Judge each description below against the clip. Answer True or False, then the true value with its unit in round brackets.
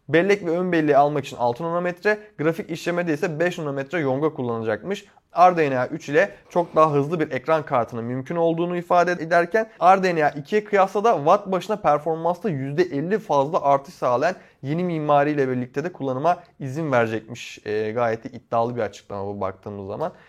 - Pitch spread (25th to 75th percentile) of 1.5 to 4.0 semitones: False (4.7 semitones)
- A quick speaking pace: True (160 wpm)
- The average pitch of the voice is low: False (155 Hz)